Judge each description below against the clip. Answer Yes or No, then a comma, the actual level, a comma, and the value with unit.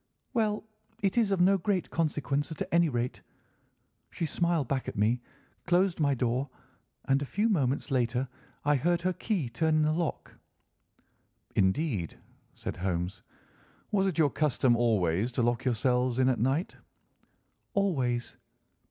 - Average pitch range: No, wide, 6.1 semitones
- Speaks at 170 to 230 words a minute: No, average, 145 wpm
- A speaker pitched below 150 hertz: Yes, medium, 140 Hz